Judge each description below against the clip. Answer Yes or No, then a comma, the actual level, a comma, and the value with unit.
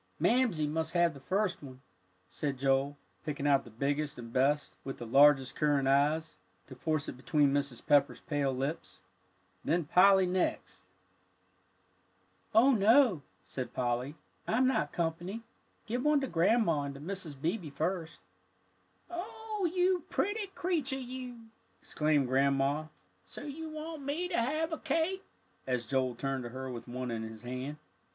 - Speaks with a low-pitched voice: No, medium, 155 Hz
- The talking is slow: No, average, 155 wpm